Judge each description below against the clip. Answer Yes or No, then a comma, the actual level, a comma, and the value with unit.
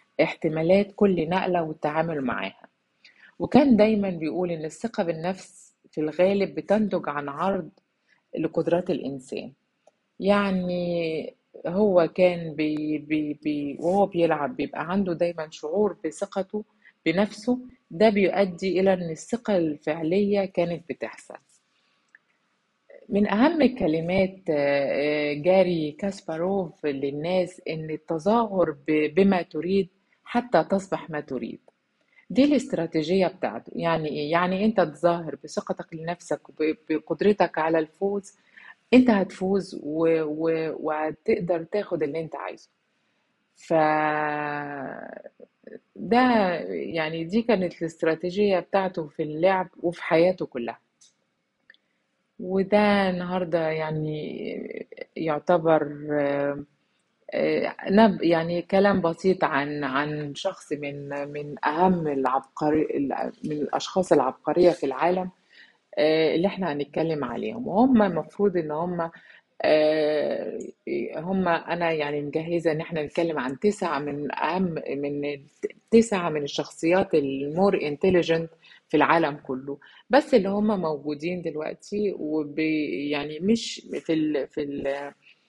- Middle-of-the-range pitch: Yes, medium, 170 Hz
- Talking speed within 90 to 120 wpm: Yes, average, 100 wpm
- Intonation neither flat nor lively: Yes, average, 4.0 semitones